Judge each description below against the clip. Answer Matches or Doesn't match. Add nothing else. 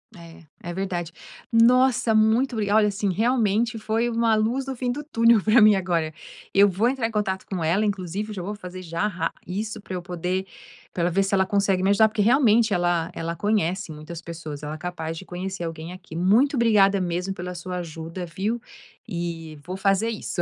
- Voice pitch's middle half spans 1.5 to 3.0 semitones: Doesn't match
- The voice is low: Doesn't match